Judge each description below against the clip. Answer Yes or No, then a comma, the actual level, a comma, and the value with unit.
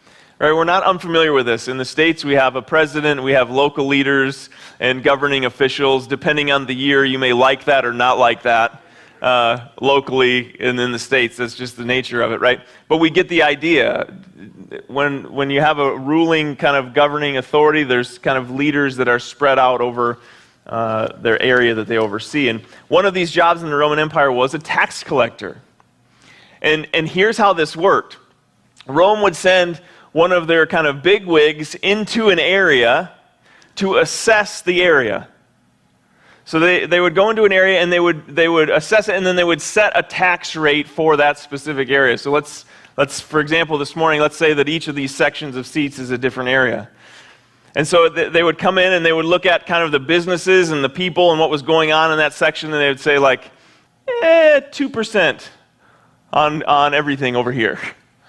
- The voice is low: No, medium, 150 Hz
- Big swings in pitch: No, average, 4.3 semitones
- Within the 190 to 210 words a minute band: Yes, average, 200 wpm